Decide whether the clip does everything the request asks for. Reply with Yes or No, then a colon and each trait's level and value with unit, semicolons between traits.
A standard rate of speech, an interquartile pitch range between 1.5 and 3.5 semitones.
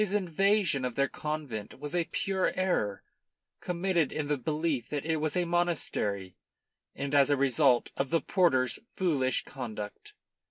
No: average, 155 wpm; average, 5.1 semitones